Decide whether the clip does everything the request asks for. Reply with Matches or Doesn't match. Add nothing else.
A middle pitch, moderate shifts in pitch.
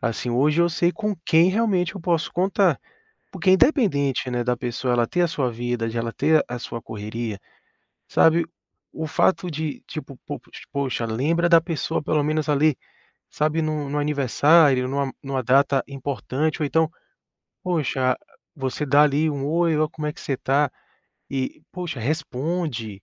Matches